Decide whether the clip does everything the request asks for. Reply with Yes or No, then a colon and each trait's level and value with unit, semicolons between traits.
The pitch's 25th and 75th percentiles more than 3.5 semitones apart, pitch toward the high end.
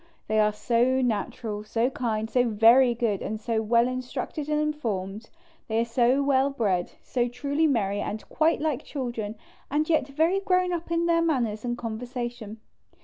Yes: average, 4.3 semitones; high, 245 Hz